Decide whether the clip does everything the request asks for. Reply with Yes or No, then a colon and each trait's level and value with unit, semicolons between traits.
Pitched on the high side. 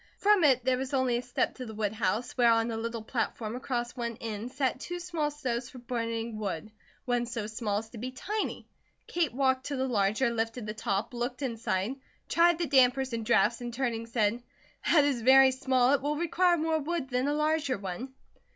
Yes: high, 245 Hz